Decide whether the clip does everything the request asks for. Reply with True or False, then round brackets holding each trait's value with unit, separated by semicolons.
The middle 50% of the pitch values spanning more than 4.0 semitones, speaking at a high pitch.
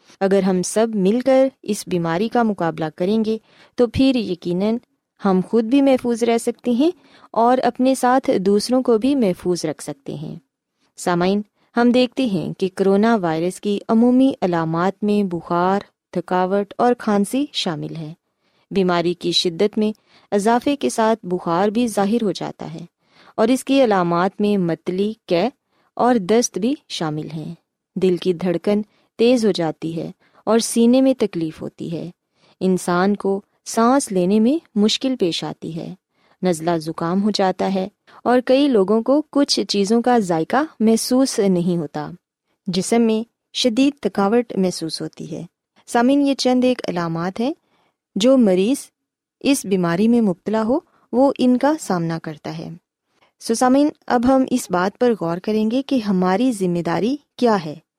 True (5.4 semitones; 210 Hz)